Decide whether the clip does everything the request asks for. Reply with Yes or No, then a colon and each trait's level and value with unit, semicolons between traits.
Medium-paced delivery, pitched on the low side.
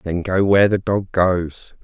Yes: average, 195 wpm; very low, 95 Hz